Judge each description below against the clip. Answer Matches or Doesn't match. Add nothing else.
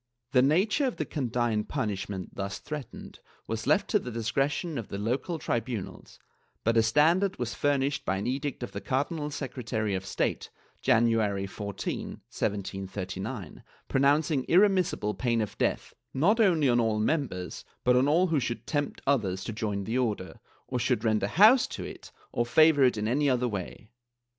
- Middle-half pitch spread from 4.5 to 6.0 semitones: Matches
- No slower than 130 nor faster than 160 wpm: Doesn't match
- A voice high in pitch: Doesn't match